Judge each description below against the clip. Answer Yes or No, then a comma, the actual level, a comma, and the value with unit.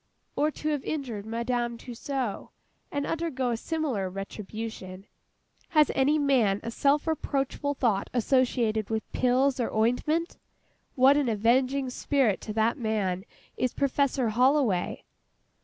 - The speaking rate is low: Yes, slow, 125 wpm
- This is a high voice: Yes, very high, 250 Hz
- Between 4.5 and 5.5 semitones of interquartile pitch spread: No, average, 4.1 semitones